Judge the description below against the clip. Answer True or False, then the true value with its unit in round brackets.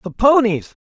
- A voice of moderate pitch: False (215 Hz)